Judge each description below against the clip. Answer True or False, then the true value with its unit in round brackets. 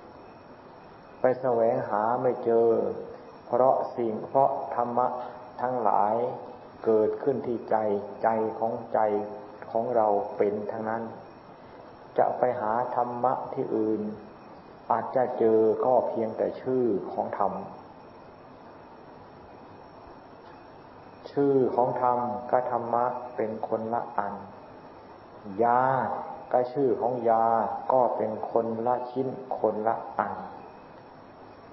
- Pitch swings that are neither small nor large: False (1.9 semitones)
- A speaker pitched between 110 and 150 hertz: True (120 Hz)